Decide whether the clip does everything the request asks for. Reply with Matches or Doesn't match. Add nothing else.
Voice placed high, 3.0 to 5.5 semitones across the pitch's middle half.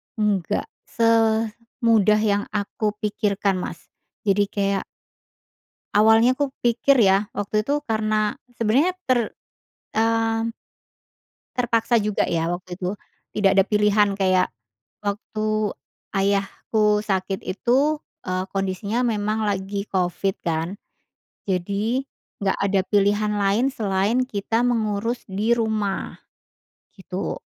Doesn't match